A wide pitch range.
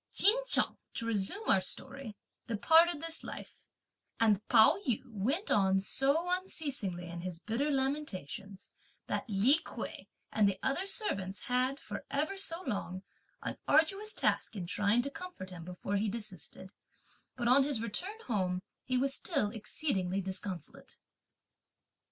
Yes: wide, 7.4 semitones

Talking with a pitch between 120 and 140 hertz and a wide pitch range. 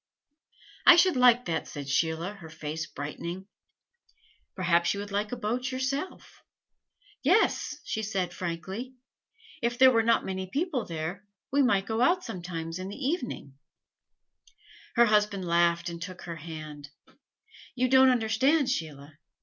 No: high, 200 Hz; wide, 7.0 semitones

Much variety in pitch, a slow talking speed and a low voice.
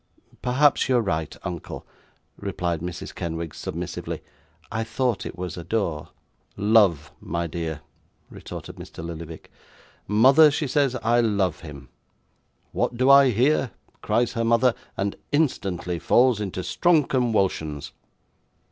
Yes: wide, 6.8 semitones; slow, 125 wpm; low, 105 Hz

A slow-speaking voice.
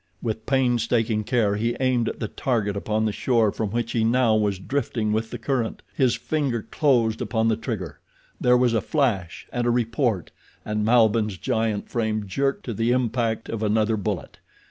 No: average, 175 wpm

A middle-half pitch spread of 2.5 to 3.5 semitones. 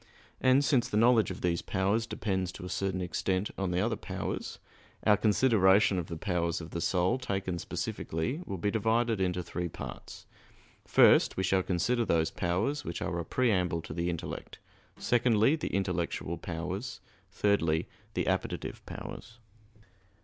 No: average, 4.1 semitones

